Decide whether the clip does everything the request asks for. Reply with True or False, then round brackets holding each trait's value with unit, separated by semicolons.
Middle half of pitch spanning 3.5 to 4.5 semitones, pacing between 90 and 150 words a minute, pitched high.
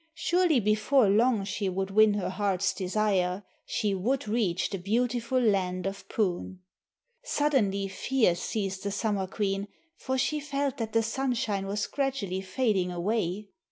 True (3.9 semitones; 145 wpm; 205 Hz)